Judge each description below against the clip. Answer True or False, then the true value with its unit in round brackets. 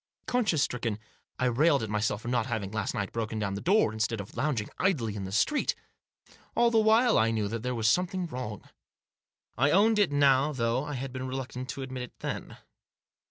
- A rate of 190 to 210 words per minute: True (205 wpm)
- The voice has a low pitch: True (125 Hz)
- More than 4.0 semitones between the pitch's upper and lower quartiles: True (5.6 semitones)